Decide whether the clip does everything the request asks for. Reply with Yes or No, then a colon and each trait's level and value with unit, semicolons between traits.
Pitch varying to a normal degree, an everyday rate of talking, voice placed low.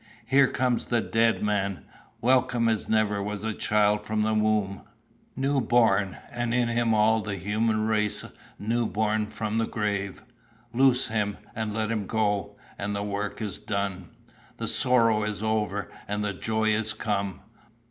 No: narrow, 1.8 semitones; average, 155 wpm; low, 110 Hz